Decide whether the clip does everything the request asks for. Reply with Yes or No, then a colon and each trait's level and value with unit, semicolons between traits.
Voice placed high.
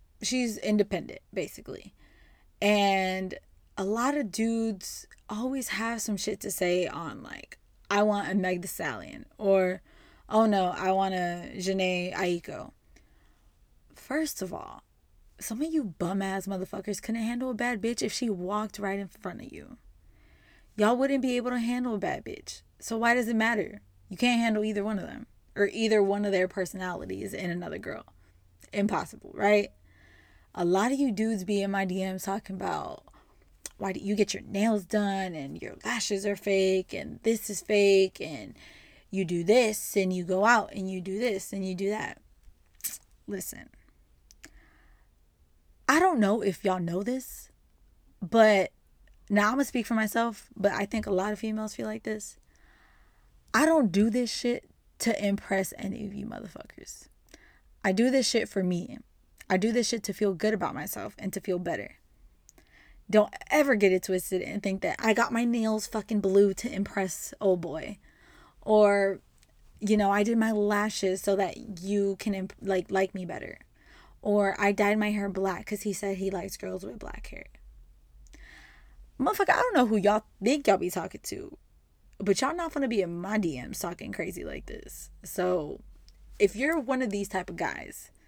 Yes: high, 200 Hz